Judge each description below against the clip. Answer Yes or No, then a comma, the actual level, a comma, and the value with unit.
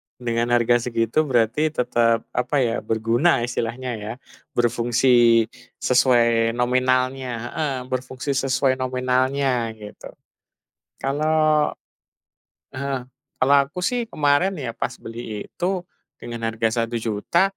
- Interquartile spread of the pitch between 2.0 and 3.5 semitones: Yes, average, 2.9 semitones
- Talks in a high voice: No, low, 125 Hz